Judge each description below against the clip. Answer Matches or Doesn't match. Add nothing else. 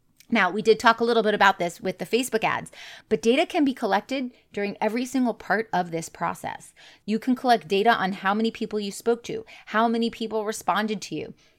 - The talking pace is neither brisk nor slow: Doesn't match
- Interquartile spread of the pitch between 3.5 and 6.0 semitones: Doesn't match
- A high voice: Matches